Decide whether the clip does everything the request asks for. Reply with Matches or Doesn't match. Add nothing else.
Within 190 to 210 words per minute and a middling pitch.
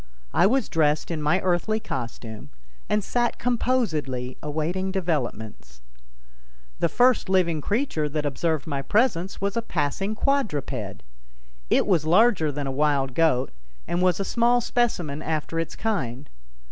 Doesn't match